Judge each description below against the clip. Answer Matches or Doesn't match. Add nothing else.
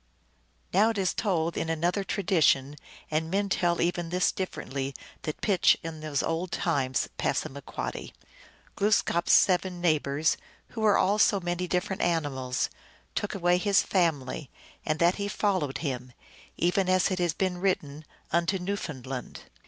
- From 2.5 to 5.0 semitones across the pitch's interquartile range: Matches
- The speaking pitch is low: Doesn't match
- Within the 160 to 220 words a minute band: Doesn't match